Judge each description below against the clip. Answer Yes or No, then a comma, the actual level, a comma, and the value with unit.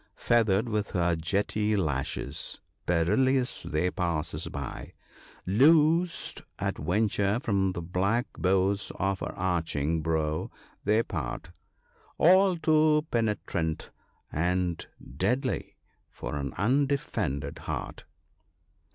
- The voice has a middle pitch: No, very low, 95 Hz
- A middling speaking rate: No, slow, 100 wpm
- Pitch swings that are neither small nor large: No, wide, 6.2 semitones